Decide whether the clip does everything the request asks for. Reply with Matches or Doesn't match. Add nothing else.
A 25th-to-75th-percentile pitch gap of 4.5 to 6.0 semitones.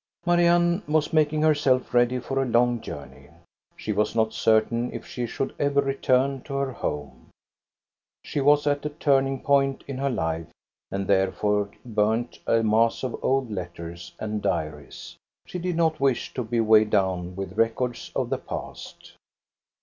Matches